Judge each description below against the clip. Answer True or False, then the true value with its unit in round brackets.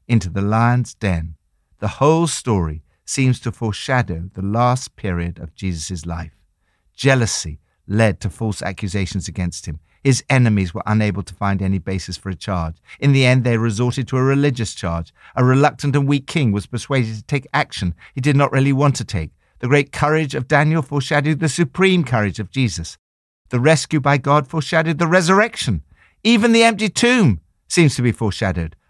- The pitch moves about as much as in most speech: False (7.5 semitones)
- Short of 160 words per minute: False (180 wpm)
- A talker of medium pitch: False (115 Hz)